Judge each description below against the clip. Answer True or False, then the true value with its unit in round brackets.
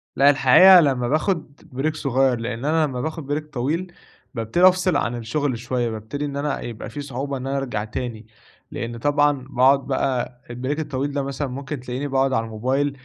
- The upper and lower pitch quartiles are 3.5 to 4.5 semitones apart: False (2.8 semitones)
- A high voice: False (135 Hz)